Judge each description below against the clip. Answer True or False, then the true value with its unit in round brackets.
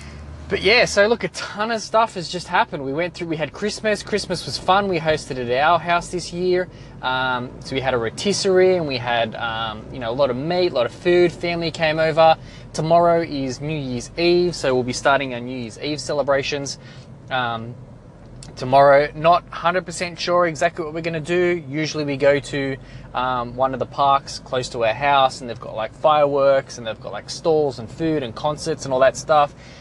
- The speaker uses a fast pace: True (215 wpm)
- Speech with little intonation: False (5.0 semitones)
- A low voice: False (145 Hz)